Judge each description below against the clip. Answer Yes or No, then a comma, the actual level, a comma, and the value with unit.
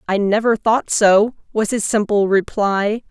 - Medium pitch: No, high, 210 Hz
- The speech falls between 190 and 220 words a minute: No, average, 155 wpm